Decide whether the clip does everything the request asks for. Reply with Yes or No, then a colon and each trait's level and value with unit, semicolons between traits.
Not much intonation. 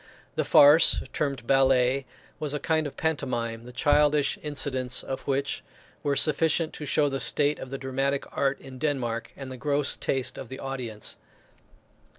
Yes: narrow, 2.1 semitones